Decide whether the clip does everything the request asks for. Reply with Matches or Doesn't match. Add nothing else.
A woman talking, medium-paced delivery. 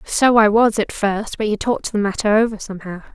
Doesn't match